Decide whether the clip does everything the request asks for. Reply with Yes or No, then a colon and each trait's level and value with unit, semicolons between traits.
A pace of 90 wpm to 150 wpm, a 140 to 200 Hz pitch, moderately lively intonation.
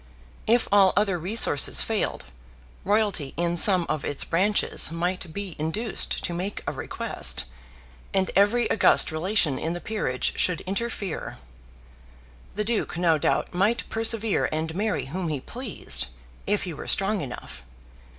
Yes: average, 140 wpm; medium, 185 Hz; average, 4.3 semitones